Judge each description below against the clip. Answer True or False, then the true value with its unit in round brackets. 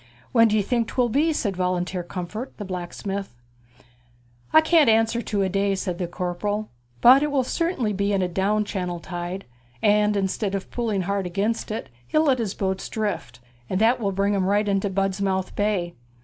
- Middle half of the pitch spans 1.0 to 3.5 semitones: True (2.9 semitones)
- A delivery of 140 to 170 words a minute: False (185 wpm)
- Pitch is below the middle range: False (200 Hz)